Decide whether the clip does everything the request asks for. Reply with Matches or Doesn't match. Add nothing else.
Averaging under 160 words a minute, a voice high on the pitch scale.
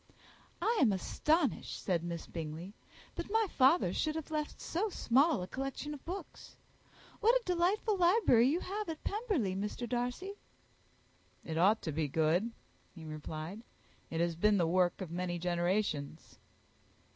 Matches